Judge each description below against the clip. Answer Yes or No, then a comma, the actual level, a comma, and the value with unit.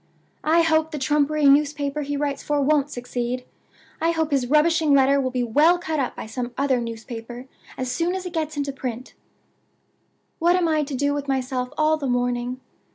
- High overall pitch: Yes, very high, 280 Hz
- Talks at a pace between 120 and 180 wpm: No, average, 190 wpm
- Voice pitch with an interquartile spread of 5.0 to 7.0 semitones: No, average, 3.5 semitones